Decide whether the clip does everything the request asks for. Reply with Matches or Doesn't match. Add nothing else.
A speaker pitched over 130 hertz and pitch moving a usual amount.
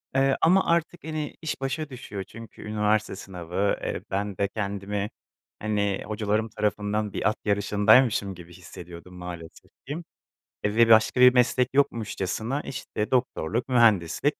Doesn't match